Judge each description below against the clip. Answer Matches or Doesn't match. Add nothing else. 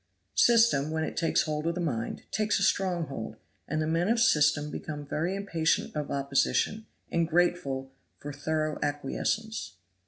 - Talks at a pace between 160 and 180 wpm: Matches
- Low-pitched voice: Doesn't match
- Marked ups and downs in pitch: Doesn't match